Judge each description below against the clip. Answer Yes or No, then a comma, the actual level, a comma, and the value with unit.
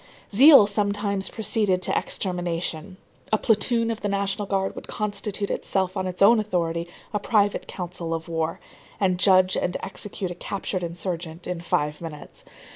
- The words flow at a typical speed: Yes, average, 155 wpm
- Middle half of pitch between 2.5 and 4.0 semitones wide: Yes, average, 2.9 semitones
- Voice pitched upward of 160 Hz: Yes, high, 190 Hz